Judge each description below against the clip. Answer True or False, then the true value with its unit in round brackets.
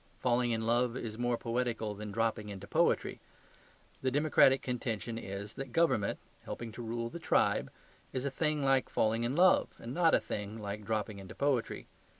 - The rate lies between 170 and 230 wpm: True (175 wpm)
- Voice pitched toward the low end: True (115 Hz)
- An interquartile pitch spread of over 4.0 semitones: False (3.3 semitones)